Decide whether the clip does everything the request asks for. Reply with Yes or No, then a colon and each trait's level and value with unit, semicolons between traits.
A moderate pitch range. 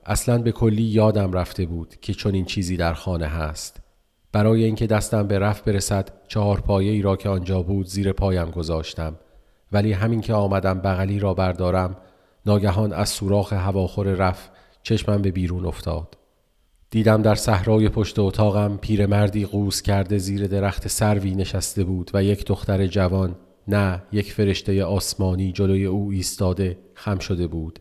No: narrow, 1.9 semitones